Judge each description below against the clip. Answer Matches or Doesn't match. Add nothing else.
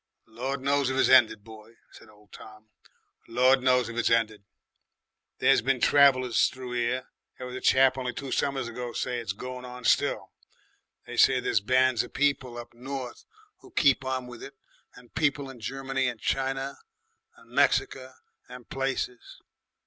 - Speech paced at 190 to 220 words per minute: Doesn't match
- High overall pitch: Doesn't match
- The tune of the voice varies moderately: Doesn't match